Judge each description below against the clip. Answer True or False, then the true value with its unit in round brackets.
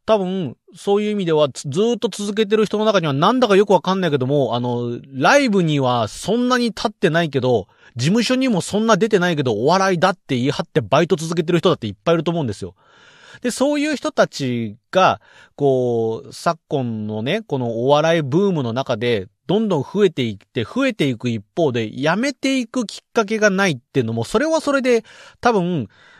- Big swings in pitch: True (8.7 semitones)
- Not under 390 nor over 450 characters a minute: True (395 characters per minute)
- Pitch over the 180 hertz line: False (175 Hz)